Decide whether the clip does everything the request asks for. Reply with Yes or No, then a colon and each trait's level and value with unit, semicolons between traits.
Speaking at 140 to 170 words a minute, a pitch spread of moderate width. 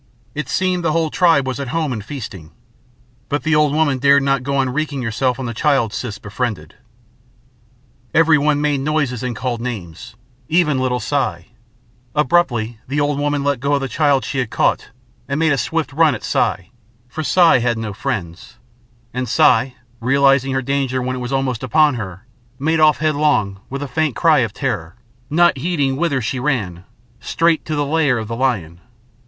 No: average, 185 wpm; average, 3.8 semitones